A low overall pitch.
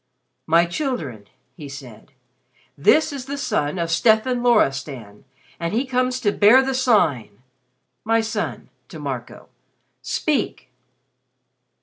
No: high, 210 Hz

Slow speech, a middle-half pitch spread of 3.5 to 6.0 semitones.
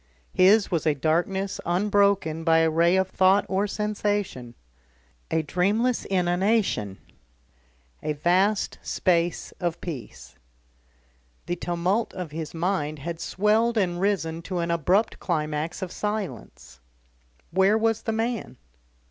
Yes: slow, 125 wpm; average, 3.9 semitones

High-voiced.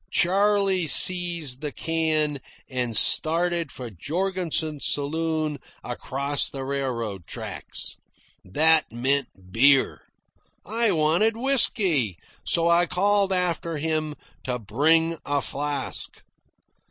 No: medium, 155 Hz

